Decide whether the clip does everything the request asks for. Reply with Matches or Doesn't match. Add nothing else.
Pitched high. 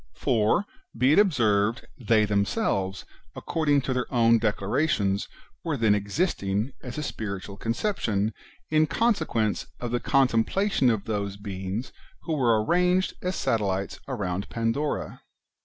Doesn't match